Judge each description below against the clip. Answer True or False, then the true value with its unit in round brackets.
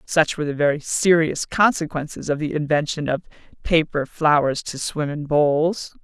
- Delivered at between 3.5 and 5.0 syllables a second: True (4.8 syllables/s)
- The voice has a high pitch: False (150 Hz)